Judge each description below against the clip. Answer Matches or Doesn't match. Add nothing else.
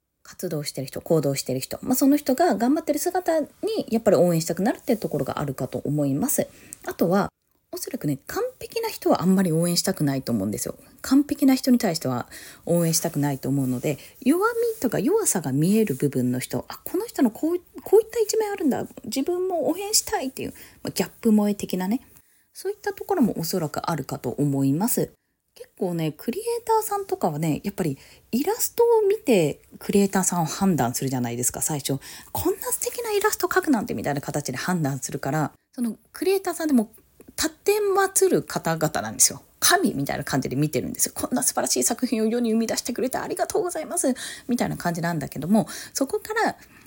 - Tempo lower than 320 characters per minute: Doesn't match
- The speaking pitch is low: Doesn't match